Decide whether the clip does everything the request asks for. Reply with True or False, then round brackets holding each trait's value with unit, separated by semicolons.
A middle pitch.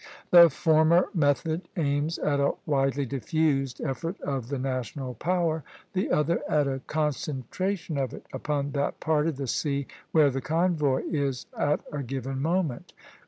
True (145 Hz)